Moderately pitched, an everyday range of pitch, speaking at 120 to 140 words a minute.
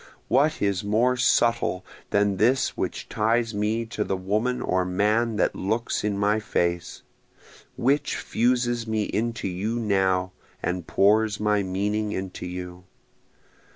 No: low, 105 Hz; average, 3.4 semitones; slow, 135 wpm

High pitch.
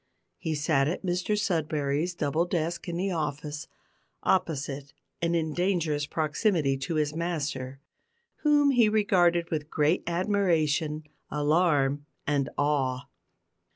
No: medium, 155 Hz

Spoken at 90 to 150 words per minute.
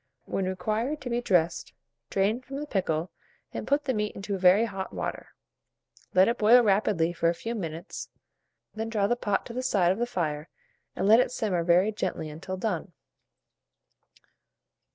No: average, 175 wpm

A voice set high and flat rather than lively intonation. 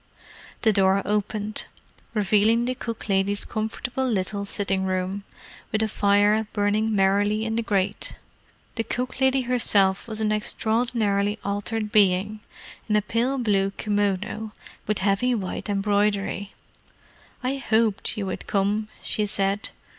Yes: high, 210 Hz; narrow, 1.9 semitones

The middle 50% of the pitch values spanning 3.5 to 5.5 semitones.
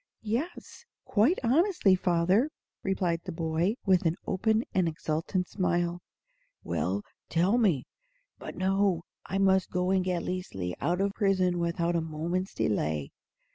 No: average, 2.7 semitones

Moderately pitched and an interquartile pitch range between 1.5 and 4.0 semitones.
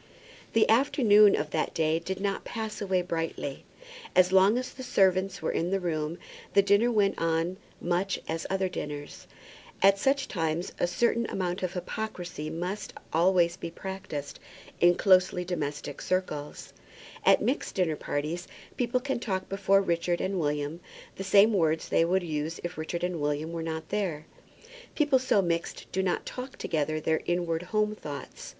Yes: medium, 180 Hz; average, 3.4 semitones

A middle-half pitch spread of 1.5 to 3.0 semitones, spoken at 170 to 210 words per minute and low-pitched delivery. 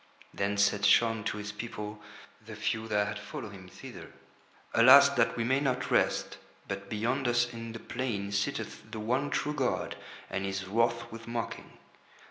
Yes: average, 2.7 semitones; average, 175 wpm; low, 110 Hz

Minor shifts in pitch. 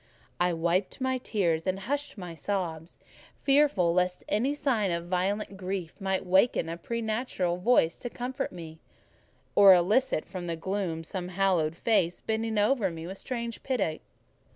No: average, 4.7 semitones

